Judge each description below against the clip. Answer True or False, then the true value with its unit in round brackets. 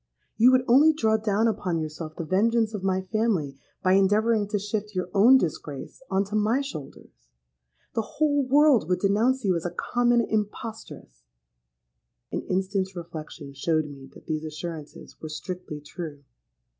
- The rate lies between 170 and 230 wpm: False (155 wpm)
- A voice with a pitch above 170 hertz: True (190 Hz)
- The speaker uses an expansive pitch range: True (6.2 semitones)